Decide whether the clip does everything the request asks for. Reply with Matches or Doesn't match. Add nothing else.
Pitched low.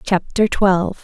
Doesn't match